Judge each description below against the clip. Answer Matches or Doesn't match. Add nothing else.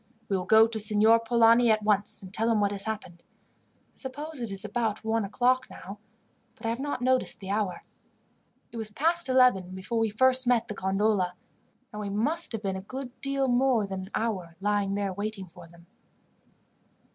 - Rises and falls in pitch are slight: Doesn't match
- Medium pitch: Doesn't match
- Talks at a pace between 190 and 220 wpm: Matches